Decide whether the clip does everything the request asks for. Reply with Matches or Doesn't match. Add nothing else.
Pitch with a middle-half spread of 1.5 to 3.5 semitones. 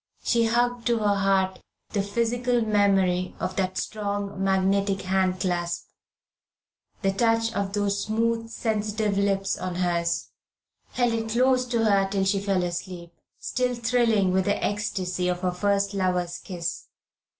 Matches